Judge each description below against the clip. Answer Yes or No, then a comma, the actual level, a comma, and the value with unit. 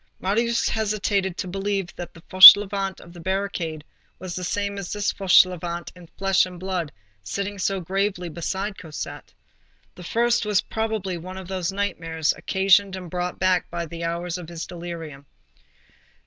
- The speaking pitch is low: No, medium, 185 Hz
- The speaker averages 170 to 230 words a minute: No, average, 155 wpm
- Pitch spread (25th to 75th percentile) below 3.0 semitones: Yes, narrow, 2.5 semitones